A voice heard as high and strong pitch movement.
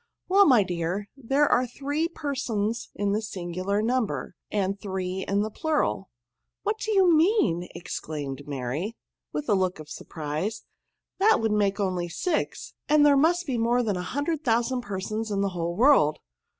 Yes: high, 215 Hz; wide, 7.3 semitones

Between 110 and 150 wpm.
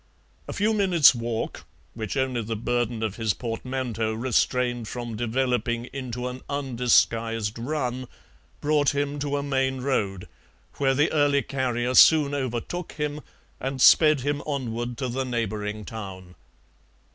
Yes: slow, 135 wpm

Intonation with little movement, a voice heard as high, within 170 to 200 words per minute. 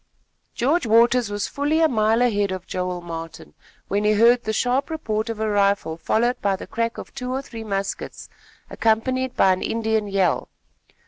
No: average, 3.7 semitones; high, 220 Hz; average, 180 wpm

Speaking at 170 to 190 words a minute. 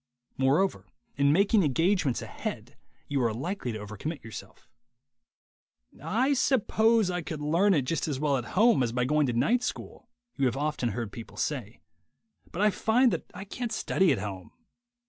Yes: average, 175 wpm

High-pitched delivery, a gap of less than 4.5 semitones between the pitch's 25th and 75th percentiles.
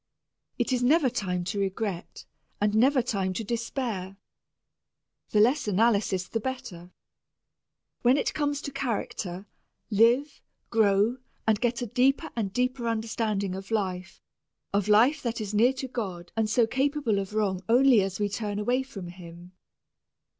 Yes: high, 220 Hz; average, 4.1 semitones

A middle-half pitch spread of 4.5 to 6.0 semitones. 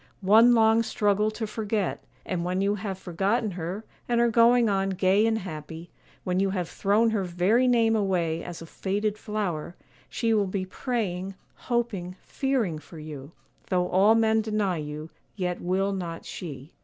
No: average, 3.7 semitones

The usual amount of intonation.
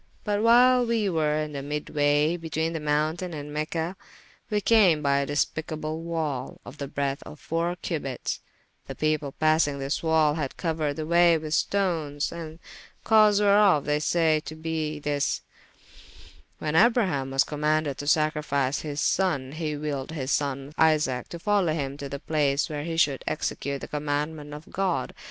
No: narrow, 2.3 semitones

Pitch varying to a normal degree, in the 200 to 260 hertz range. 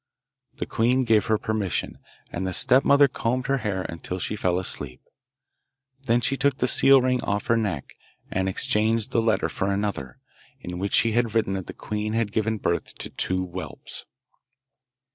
No: average, 3.8 semitones; low, 110 Hz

